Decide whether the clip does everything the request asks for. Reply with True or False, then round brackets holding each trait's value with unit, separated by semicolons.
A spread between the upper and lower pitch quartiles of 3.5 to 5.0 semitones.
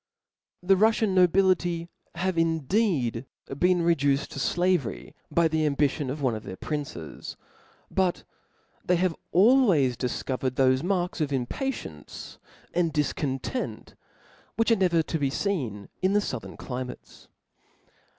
False (5.6 semitones)